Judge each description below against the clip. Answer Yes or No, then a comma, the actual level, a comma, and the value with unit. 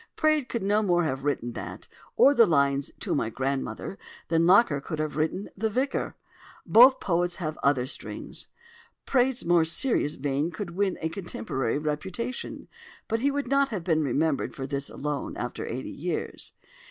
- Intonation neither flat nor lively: No, wide, 7.3 semitones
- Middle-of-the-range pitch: Yes, medium, 165 Hz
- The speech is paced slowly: No, average, 165 wpm